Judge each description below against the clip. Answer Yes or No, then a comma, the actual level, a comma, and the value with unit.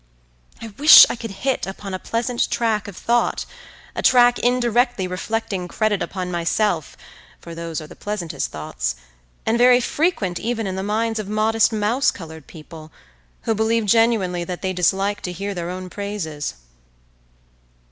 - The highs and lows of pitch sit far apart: No, average, 4.3 semitones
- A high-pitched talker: Yes, high, 205 Hz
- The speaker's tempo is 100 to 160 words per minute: Yes, average, 155 wpm